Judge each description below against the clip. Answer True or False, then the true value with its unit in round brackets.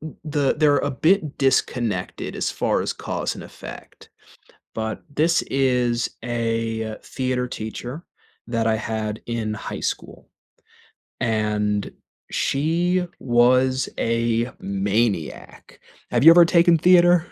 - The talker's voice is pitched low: True (120 Hz)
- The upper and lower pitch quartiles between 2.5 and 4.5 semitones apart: False (4.9 semitones)